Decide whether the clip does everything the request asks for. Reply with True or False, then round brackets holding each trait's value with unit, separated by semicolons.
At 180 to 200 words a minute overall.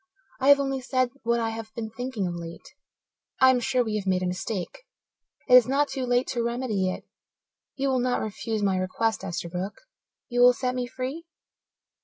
True (195 wpm)